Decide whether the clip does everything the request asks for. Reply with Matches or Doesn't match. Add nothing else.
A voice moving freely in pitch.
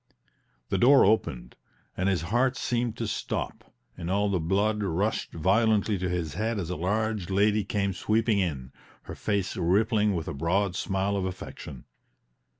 Doesn't match